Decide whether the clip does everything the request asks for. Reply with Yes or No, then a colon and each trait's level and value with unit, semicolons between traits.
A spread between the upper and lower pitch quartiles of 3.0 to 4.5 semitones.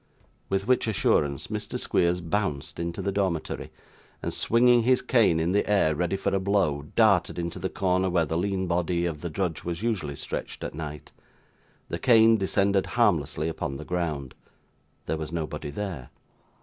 Yes: average, 3.8 semitones